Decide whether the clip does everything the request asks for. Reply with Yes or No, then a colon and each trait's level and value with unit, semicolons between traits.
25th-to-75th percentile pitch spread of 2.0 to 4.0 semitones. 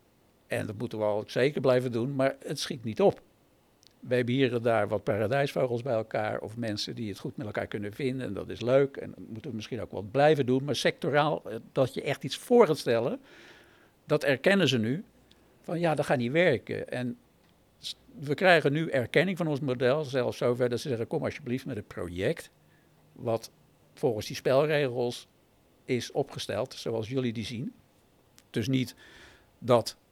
Yes: average, 3.7 semitones